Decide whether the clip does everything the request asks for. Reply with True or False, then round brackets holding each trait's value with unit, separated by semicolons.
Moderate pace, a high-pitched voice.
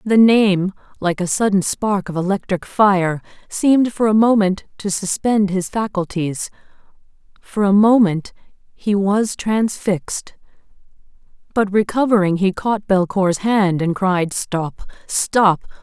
False (120 wpm; 195 Hz)